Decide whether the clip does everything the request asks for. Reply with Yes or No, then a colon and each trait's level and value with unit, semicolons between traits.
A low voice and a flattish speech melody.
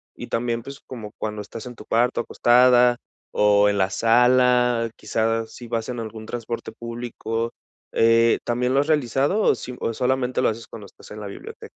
Yes: low, 115 Hz; narrow, 1.8 semitones